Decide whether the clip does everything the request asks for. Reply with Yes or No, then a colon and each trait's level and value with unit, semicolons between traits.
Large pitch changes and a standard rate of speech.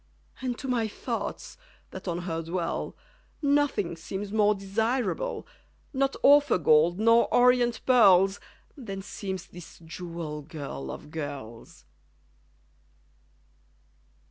No: wide, 6.5 semitones; slow, 105 wpm